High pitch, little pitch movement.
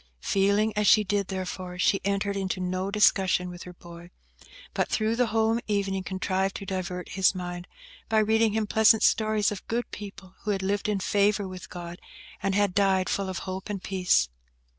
Yes: high, 195 Hz; narrow, 2.1 semitones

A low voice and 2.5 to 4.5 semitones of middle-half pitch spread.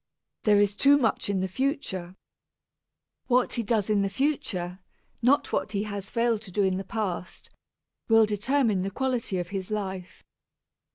No: high, 205 Hz; average, 3.7 semitones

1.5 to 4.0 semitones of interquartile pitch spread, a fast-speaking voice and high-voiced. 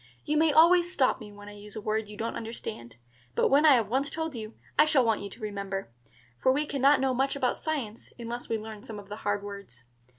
No: average, 5.1 semitones; fast, 245 wpm; high, 230 Hz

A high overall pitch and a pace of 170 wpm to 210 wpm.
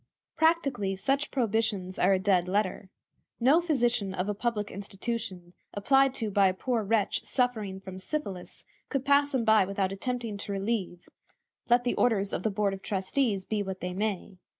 Yes: high, 205 Hz; average, 175 wpm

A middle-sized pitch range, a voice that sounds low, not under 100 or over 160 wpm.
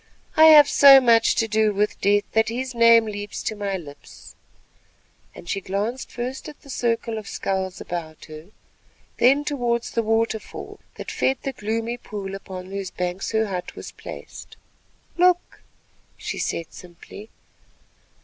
No: average, 3.6 semitones; high, 220 Hz; average, 150 wpm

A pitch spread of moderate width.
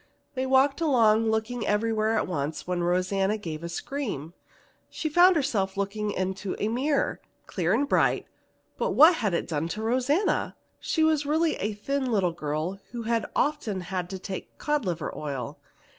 No: wide, 6.9 semitones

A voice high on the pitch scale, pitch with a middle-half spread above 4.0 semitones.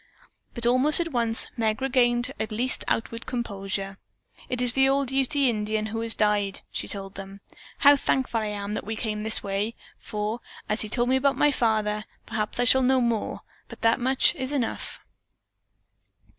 No: high, 230 Hz; average, 3.4 semitones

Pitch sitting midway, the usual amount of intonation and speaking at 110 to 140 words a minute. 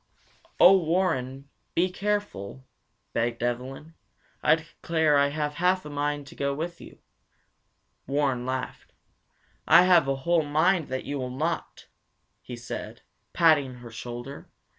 Yes: medium, 145 Hz; average, 4.3 semitones; slow, 135 wpm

